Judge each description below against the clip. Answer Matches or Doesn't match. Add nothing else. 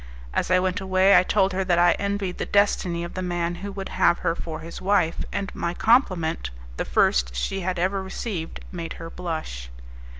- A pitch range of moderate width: Doesn't match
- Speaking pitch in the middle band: Matches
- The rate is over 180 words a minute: Matches